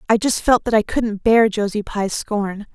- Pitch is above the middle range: Yes, high, 215 Hz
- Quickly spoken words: Yes, fast, 220 wpm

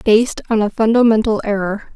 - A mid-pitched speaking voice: No, high, 215 Hz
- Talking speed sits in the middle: Yes, average, 155 wpm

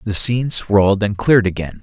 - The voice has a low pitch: Yes, low, 105 Hz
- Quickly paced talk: No, average, 195 wpm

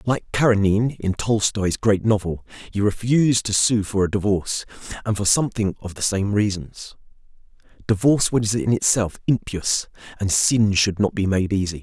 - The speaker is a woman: No, male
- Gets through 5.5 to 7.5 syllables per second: No, 5.1 syllables/s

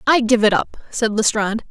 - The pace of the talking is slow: No, fast, 210 wpm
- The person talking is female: Yes, female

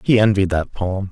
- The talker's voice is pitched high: No, low, 100 Hz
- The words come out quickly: Yes, fast, 215 wpm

